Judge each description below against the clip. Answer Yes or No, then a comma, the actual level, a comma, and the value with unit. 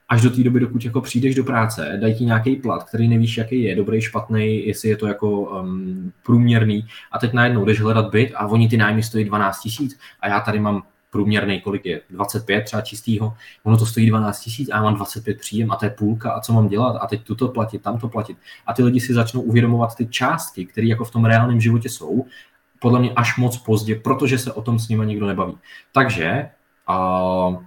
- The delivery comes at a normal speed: No, fast, 220 wpm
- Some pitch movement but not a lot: No, narrow, 2.2 semitones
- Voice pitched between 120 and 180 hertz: No, low, 110 Hz